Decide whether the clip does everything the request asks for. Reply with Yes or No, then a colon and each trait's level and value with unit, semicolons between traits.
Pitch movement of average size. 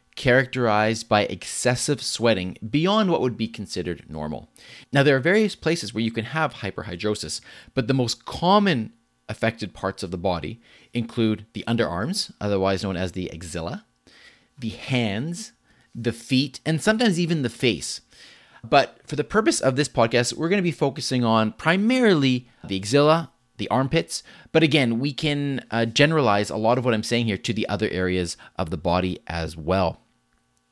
No: wide, 7.0 semitones